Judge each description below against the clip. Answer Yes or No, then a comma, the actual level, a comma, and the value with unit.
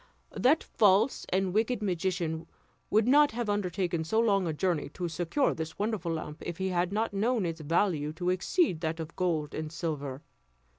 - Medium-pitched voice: Yes, medium, 180 Hz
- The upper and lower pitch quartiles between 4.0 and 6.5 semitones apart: Yes, average, 4.4 semitones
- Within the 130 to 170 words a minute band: No, average, 180 wpm